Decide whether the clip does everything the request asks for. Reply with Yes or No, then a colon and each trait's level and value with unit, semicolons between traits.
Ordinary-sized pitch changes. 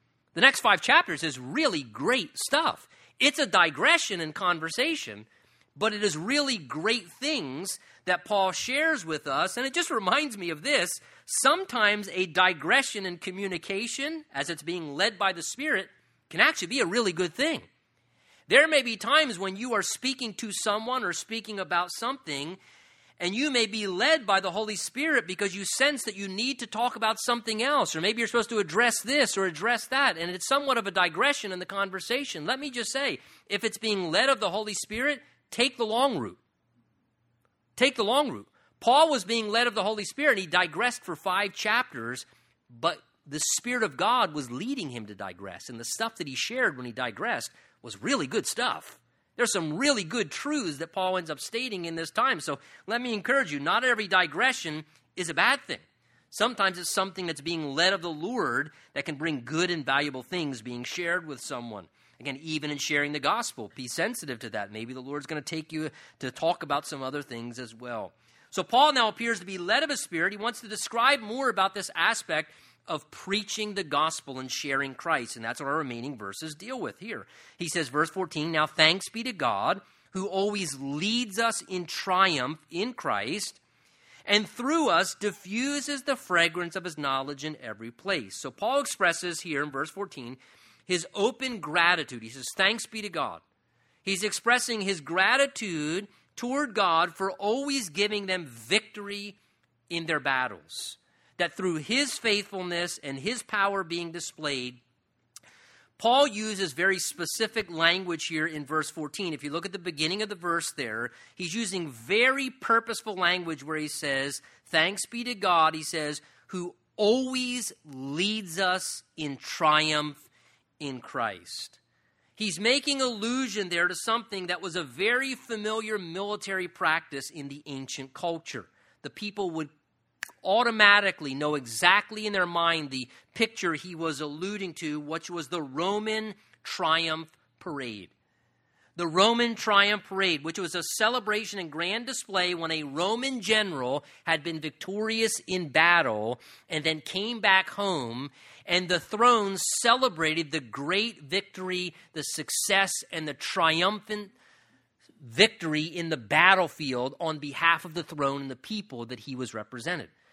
No: wide, 6.0 semitones